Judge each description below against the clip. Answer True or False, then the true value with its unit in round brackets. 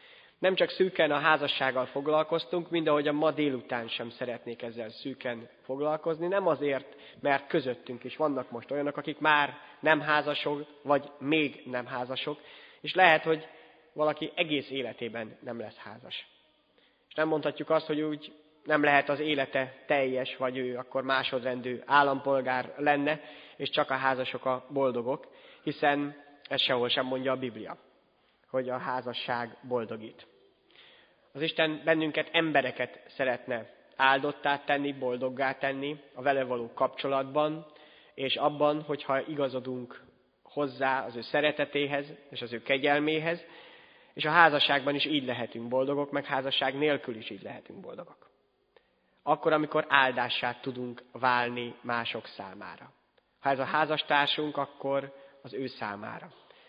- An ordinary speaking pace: True (135 wpm)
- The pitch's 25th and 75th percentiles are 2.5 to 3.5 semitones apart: True (2.8 semitones)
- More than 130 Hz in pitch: True (140 Hz)